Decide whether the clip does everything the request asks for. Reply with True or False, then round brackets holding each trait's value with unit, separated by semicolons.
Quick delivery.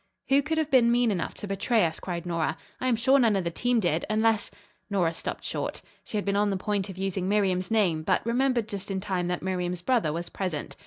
True (245 wpm)